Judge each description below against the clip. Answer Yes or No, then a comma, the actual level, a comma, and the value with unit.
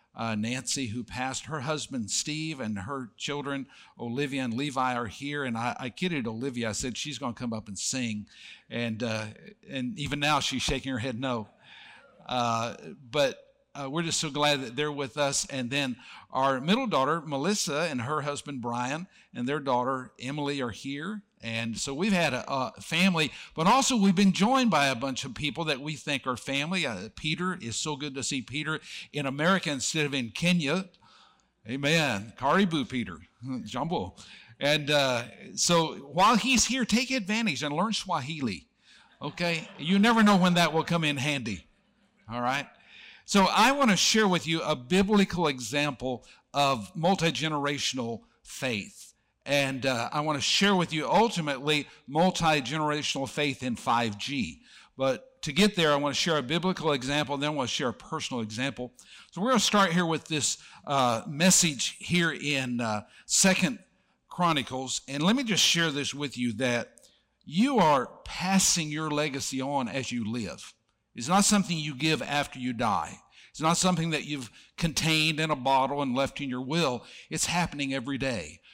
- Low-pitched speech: No, medium, 145 Hz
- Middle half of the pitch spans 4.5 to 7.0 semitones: Yes, average, 4.8 semitones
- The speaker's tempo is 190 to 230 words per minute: No, average, 180 wpm